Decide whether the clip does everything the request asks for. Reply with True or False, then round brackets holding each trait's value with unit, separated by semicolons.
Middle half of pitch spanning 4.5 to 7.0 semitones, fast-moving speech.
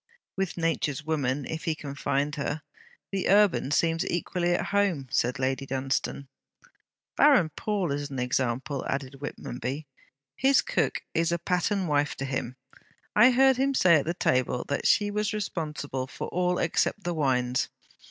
False (5.2 semitones; 155 wpm)